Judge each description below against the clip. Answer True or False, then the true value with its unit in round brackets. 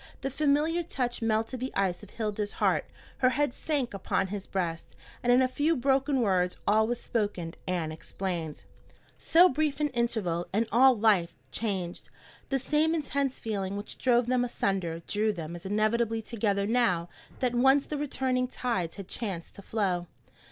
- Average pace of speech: True (165 wpm)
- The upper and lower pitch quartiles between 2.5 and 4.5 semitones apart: False (5.3 semitones)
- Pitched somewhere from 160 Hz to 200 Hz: False (225 Hz)